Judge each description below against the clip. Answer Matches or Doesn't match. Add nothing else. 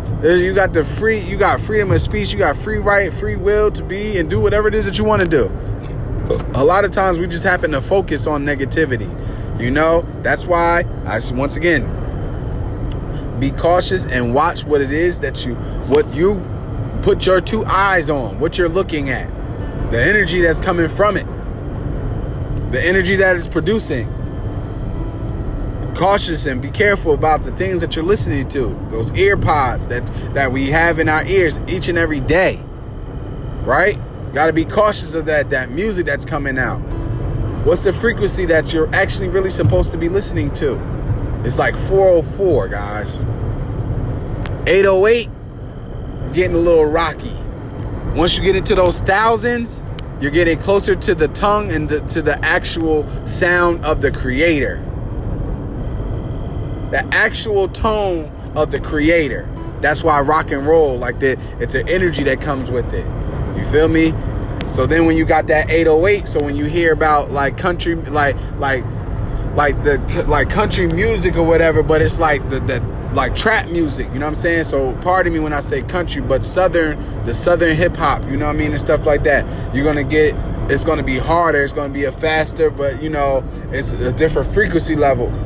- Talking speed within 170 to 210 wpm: Matches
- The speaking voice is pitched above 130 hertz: Matches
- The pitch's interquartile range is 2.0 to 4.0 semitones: Doesn't match